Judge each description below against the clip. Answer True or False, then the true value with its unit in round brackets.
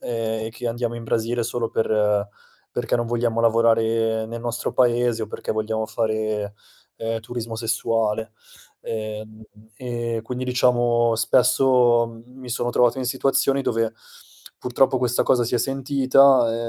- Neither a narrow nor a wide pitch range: False (1.5 semitones)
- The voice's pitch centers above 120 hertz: False (115 Hz)